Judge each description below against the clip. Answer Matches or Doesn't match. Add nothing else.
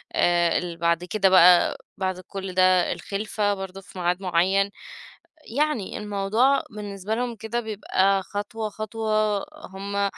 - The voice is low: Doesn't match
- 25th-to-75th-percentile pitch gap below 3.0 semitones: Matches